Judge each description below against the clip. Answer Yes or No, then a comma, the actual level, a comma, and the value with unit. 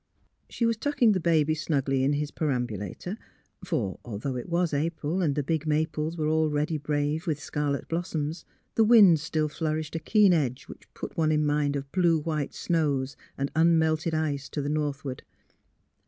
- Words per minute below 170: No, average, 180 wpm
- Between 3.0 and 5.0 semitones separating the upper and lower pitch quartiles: No, narrow, 2.4 semitones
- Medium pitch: Yes, medium, 155 Hz